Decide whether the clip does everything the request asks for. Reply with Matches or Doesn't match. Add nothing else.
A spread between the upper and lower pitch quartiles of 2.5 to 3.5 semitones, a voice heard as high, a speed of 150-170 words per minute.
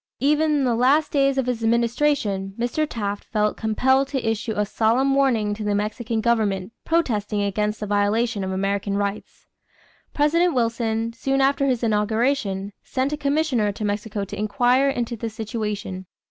Doesn't match